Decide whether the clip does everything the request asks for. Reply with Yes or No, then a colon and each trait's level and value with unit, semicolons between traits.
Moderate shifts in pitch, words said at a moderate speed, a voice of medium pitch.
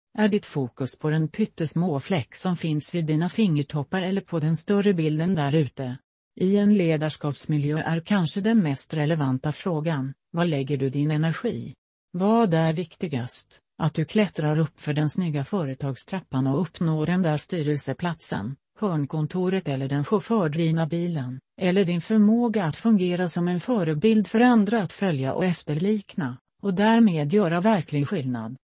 Yes: average, 4.7 semitones; average, 150 wpm; medium, 165 Hz